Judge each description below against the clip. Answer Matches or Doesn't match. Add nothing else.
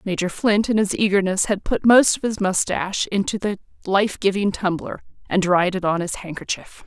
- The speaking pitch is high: Matches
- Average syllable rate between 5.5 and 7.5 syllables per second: Doesn't match